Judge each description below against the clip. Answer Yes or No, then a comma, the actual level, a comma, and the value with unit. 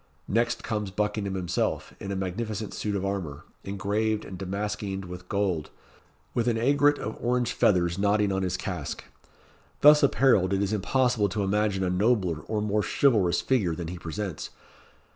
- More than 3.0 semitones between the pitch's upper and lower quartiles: No, average, 2.7 semitones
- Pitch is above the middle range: No, low, 100 Hz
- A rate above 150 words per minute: Yes, average, 160 wpm